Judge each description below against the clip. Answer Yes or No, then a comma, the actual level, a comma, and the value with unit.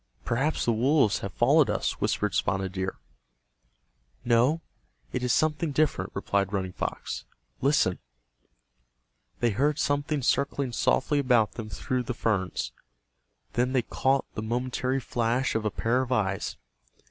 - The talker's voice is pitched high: No, low, 125 Hz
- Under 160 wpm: Yes, slow, 135 wpm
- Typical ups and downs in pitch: Yes, average, 4.3 semitones